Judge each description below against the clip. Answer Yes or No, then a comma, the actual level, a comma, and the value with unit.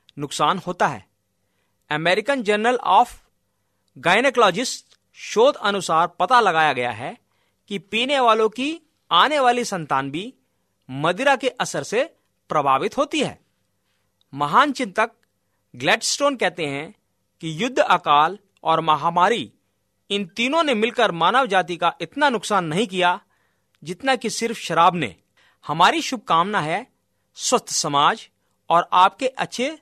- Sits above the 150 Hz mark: Yes, medium, 185 Hz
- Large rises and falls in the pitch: Yes, wide, 8.4 semitones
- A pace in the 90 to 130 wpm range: Yes, average, 125 wpm